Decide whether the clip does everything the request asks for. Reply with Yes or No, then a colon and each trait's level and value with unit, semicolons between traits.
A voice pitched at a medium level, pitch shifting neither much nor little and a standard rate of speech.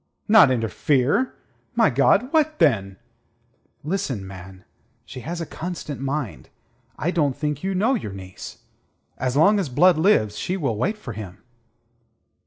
No: medium, 145 Hz; wide, 8.7 semitones; average, 145 wpm